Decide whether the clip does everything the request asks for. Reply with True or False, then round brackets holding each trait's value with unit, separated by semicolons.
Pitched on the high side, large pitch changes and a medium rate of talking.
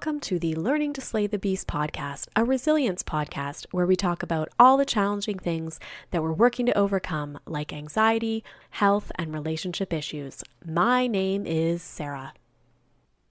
False (175 Hz; 5.9 semitones; 160 wpm)